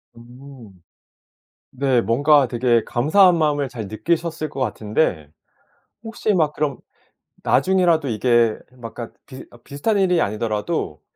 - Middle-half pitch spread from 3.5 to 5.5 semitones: Yes, average, 5.2 semitones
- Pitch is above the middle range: No, low, 135 Hz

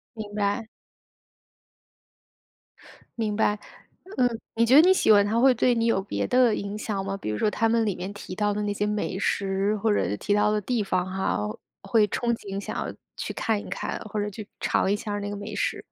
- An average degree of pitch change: No, narrow, 2.0 semitones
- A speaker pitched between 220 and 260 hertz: No, high, 210 Hz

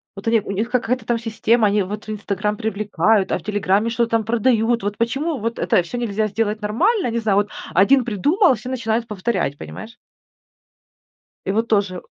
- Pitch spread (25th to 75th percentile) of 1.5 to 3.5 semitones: Yes, narrow, 2.4 semitones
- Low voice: No, high, 220 Hz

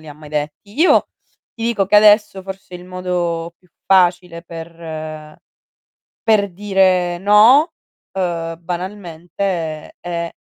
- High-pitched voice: No, medium, 180 Hz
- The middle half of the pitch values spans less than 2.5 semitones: No, average, 2.8 semitones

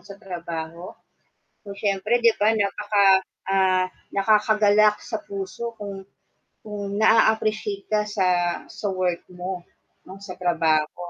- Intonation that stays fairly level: Yes, narrow, 2.3 semitones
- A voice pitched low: No, high, 200 Hz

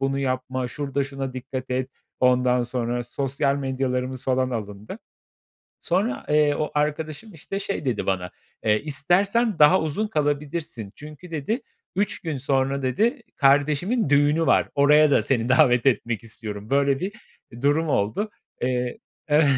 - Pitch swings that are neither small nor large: Yes, average, 3.3 semitones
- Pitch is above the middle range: No, medium, 140 Hz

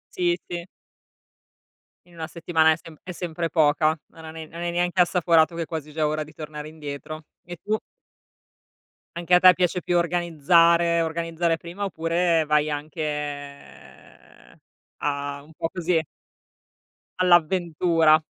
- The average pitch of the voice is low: No, medium, 165 Hz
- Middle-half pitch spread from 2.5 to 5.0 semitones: No, narrow, 2.0 semitones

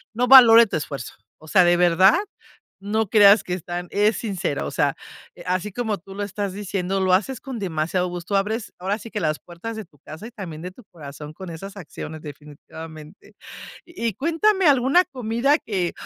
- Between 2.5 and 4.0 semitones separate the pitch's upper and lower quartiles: No, average, 4.6 semitones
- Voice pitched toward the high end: Yes, high, 195 Hz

